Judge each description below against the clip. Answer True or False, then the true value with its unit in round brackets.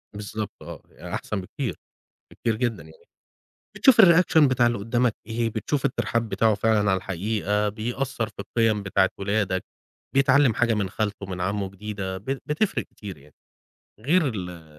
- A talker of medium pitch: False (110 Hz)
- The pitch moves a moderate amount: True (3.5 semitones)